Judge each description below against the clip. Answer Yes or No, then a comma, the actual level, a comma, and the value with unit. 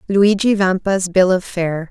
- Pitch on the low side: No, high, 190 Hz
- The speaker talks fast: No, average, 160 wpm